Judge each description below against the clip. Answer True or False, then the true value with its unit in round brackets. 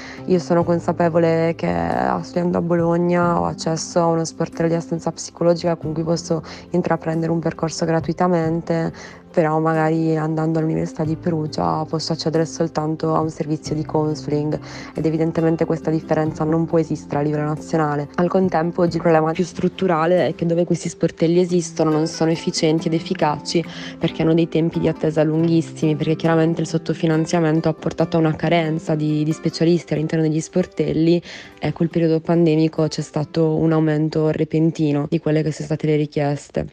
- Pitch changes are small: True (1.2 semitones)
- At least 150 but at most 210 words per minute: True (165 wpm)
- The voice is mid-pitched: True (160 Hz)